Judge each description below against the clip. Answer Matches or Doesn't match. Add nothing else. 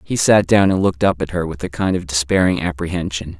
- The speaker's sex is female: Doesn't match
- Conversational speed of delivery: Doesn't match